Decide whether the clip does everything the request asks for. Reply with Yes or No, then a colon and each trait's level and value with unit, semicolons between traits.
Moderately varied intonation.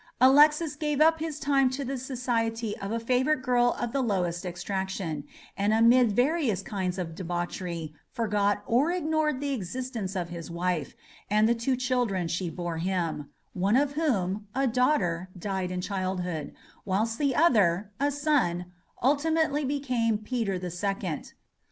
No: wide, 6.7 semitones